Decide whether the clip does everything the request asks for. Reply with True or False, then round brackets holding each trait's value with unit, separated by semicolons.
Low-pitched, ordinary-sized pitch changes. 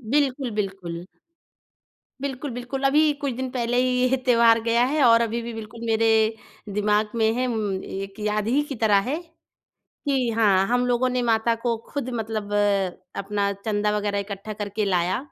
False (225 Hz; 3.2 semitones)